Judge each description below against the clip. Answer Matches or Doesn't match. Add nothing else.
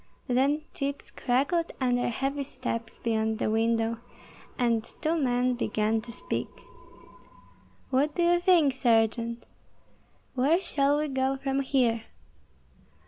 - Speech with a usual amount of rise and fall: Matches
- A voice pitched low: Doesn't match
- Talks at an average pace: Doesn't match